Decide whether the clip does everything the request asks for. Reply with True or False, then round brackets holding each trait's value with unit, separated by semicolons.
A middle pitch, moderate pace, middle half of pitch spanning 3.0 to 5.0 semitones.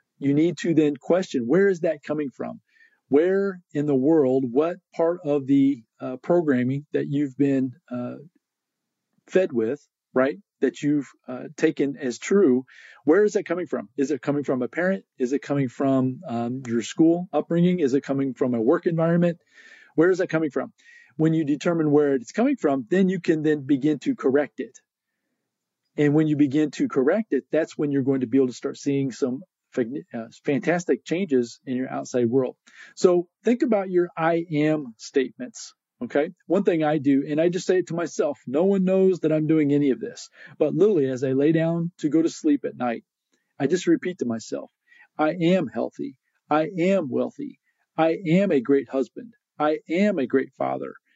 True (155 Hz; 190 wpm; 4.6 semitones)